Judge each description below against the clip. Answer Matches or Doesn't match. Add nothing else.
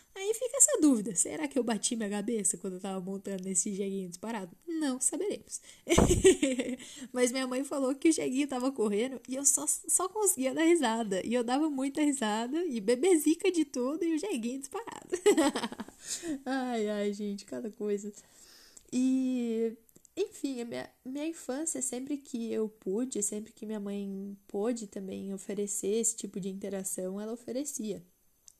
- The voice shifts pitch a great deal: Matches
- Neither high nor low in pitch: Doesn't match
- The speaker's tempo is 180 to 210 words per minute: Doesn't match